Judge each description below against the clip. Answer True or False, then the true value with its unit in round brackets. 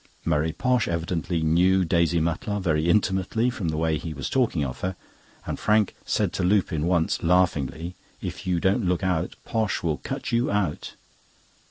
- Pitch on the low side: True (90 Hz)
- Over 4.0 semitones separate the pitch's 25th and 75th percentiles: False (3.2 semitones)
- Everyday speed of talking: True (170 wpm)